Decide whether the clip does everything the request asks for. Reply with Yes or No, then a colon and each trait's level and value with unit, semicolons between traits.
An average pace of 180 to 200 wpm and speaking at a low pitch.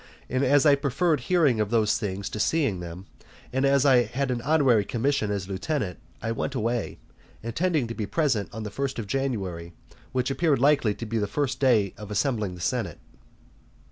Yes: average, 190 wpm; low, 120 Hz